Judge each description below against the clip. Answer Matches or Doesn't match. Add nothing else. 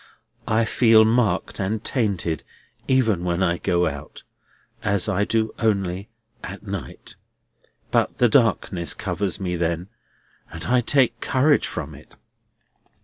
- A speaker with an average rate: Doesn't match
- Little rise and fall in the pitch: Doesn't match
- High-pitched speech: Doesn't match